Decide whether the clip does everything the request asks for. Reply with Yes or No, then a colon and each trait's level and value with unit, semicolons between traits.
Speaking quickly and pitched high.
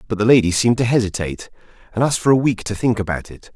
No: fast, 255 wpm; low, 110 Hz